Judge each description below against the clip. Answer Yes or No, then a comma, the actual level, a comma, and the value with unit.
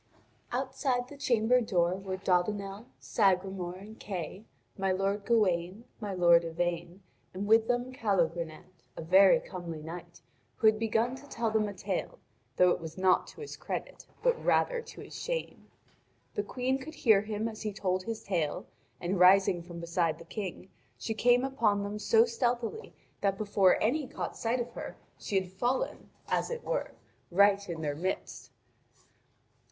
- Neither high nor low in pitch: No, high, 200 Hz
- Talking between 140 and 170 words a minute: Yes, average, 165 wpm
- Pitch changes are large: No, average, 4.3 semitones